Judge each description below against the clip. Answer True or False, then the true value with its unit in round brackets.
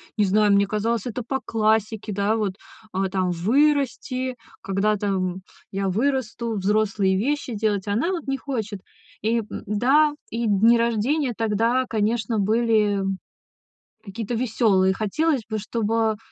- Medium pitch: False (220 Hz)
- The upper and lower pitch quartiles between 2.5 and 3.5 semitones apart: True (2.9 semitones)